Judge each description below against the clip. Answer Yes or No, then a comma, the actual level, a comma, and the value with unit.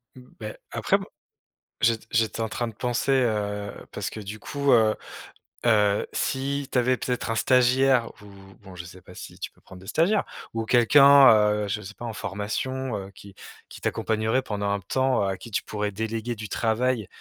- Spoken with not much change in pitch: No, average, 3.7 semitones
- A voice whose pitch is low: Yes, low, 115 Hz